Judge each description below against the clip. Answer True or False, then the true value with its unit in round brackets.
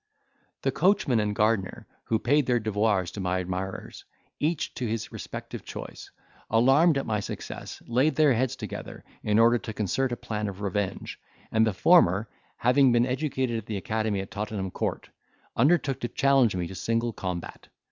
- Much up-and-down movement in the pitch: False (4.3 semitones)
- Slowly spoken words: False (170 wpm)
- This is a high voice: False (115 Hz)